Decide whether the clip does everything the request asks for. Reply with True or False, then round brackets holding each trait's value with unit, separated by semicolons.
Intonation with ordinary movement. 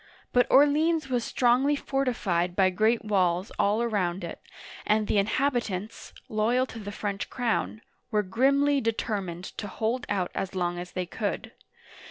True (4.7 semitones)